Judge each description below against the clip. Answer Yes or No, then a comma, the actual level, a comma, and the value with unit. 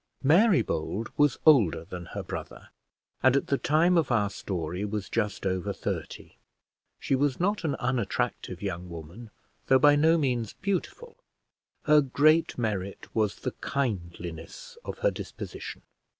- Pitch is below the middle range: Yes, low, 125 Hz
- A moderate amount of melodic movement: No, wide, 7.7 semitones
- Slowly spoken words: No, average, 145 wpm